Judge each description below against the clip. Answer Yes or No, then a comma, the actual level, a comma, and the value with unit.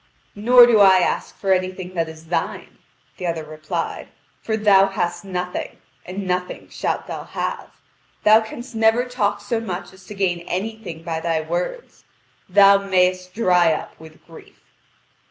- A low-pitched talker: No, medium, 185 Hz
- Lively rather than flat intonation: No, average, 3.2 semitones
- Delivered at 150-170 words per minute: Yes, average, 155 wpm